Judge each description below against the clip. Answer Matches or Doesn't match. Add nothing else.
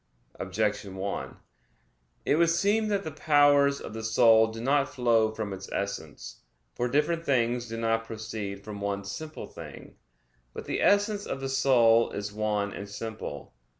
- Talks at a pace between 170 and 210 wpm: Doesn't match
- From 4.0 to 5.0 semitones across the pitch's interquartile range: Doesn't match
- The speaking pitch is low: Matches